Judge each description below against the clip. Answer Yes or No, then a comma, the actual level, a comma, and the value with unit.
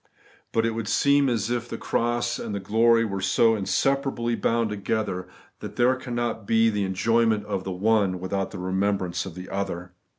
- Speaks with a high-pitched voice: No, low, 110 Hz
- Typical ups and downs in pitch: Yes, average, 3.3 semitones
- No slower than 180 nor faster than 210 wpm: Yes, average, 190 wpm